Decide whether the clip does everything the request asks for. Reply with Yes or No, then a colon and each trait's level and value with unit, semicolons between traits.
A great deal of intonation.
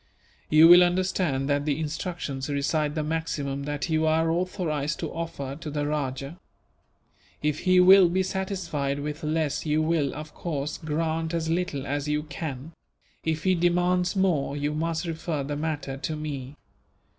No: average, 2.7 semitones